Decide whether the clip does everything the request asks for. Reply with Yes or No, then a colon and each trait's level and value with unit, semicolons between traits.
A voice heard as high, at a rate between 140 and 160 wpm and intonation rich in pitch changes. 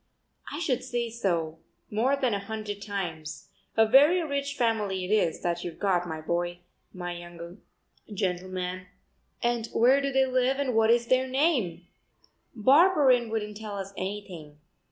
Yes: high, 210 Hz; average, 155 wpm; wide, 6.1 semitones